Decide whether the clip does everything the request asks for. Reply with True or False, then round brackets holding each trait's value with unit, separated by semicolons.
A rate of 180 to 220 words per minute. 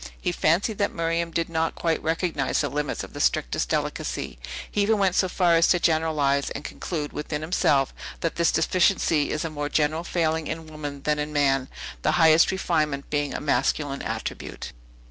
True (185 wpm)